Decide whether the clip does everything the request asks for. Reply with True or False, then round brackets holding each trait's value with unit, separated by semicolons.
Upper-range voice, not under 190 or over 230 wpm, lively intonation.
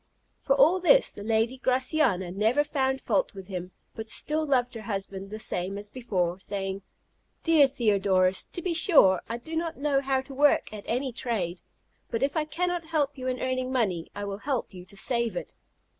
True (240 Hz; 200 wpm; 6.0 semitones)